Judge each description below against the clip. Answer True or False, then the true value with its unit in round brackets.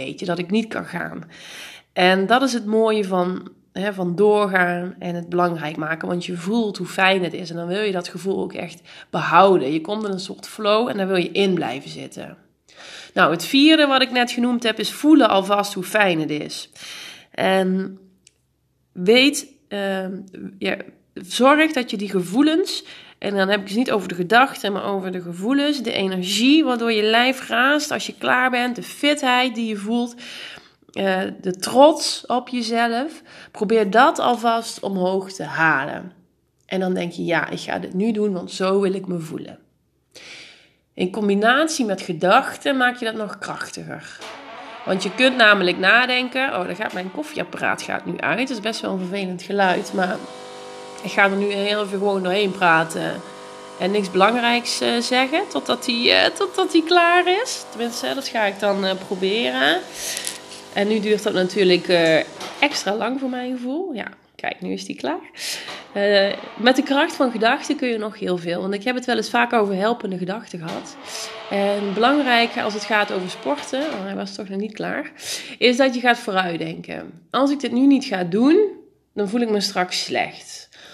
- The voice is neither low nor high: False (210 Hz)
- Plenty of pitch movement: False (4.8 semitones)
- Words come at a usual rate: True (185 wpm)